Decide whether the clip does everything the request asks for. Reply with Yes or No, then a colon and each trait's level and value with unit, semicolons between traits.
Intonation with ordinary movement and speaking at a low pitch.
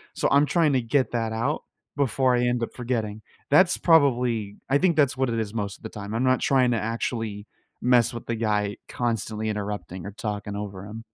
Yes: average, 3.5 semitones; low, 115 Hz